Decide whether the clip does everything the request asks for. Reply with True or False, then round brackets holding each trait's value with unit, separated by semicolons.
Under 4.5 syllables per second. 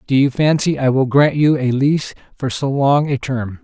False (4.9 syllables/s)